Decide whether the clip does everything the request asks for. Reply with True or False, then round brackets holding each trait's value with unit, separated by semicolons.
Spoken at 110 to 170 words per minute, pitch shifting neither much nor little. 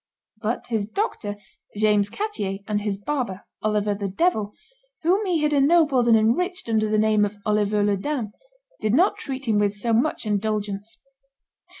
True (165 wpm; 5.0 semitones)